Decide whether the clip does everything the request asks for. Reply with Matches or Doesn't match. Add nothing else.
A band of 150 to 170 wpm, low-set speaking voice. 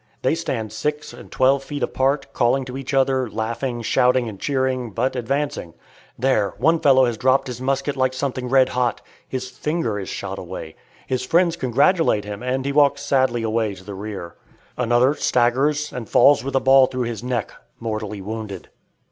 Doesn't match